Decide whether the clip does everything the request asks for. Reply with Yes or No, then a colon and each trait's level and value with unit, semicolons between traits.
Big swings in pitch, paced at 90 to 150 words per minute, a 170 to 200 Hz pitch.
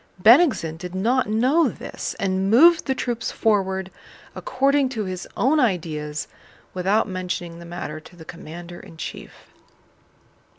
Yes: wide, 6.2 semitones; slow, 135 wpm; high, 190 Hz